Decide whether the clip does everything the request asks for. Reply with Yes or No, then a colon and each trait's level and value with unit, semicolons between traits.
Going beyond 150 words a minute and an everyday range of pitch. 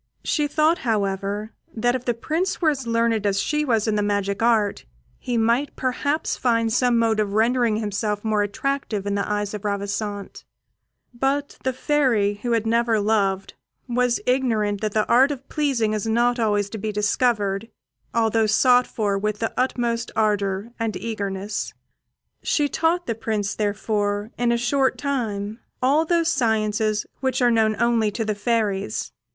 Yes: average, 165 wpm; average, 3.1 semitones